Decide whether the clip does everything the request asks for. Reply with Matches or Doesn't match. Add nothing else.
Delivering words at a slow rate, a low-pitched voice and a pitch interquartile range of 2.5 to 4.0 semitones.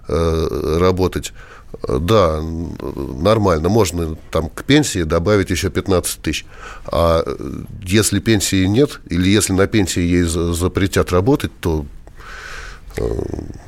Matches